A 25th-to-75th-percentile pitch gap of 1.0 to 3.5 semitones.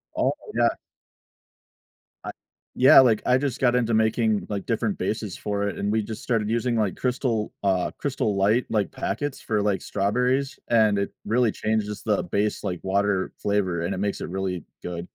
Yes: average, 2.9 semitones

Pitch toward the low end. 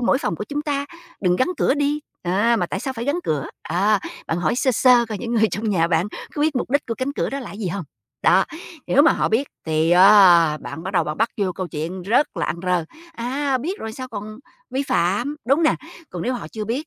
No: high, 220 Hz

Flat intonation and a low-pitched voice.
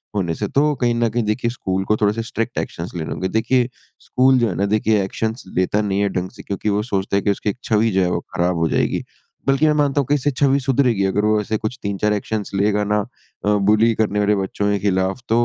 No: average, 3.1 semitones; low, 105 Hz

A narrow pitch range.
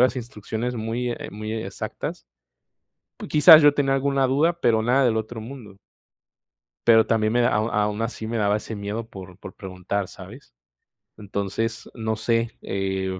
No: average, 3.1 semitones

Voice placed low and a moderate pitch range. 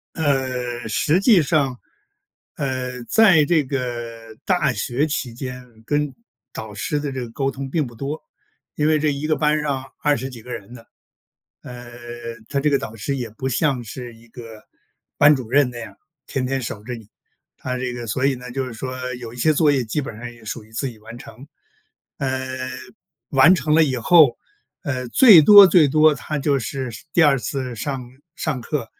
Yes: low, 130 Hz; average, 3.5 semitones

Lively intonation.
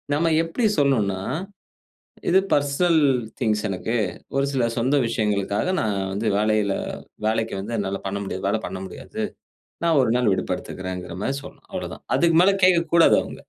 Yes: wide, 6.5 semitones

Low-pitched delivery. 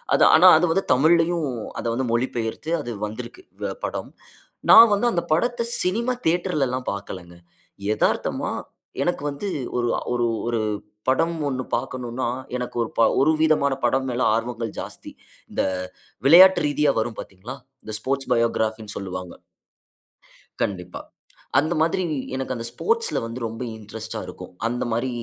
Yes: low, 130 Hz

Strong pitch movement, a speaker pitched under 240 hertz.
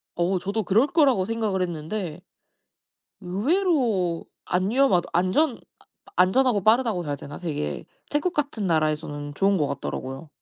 Yes: wide, 6.1 semitones; high, 190 Hz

